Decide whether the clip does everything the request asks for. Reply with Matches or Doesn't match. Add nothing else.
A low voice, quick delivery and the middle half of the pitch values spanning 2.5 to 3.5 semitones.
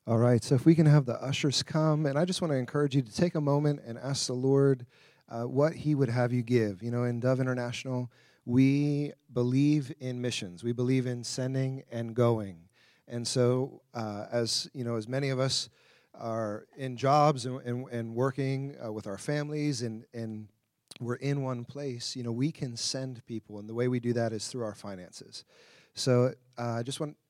Matches